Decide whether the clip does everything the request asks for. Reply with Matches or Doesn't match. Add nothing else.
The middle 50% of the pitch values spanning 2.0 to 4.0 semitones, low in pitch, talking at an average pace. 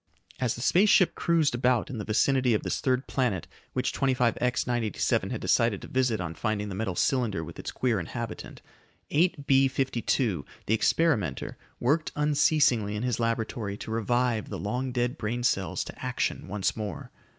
Matches